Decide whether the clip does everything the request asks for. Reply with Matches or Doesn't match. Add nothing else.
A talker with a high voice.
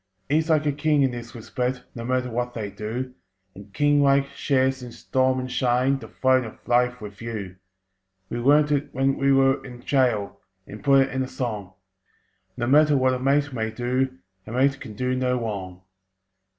Doesn't match